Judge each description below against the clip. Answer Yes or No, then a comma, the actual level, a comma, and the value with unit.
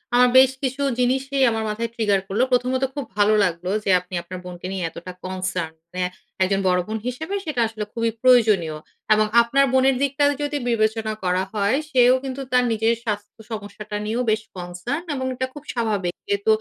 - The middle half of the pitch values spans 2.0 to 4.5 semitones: No, average, 5.1 semitones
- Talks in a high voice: Yes, high, 225 Hz